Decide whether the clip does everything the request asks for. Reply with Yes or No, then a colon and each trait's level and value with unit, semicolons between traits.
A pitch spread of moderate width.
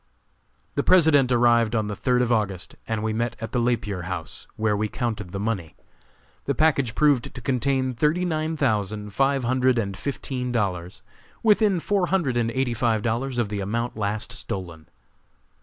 Yes: average, 4.2 semitones